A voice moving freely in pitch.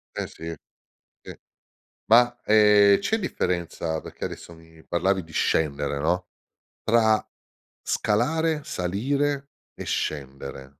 Yes: wide, 6.8 semitones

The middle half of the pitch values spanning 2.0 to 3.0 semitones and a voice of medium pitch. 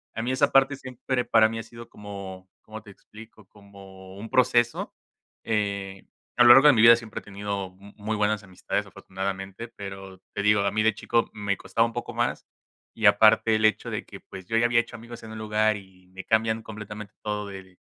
No: narrow, 2.6 semitones; low, 105 Hz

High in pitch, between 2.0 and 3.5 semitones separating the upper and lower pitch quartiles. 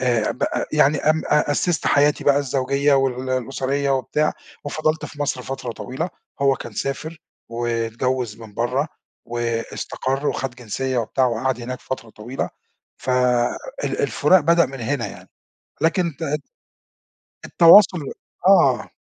No: low, 135 Hz; average, 3.2 semitones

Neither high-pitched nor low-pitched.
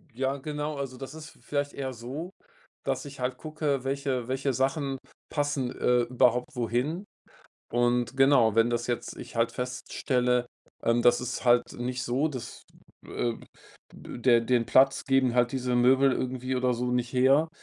No: low, 125 Hz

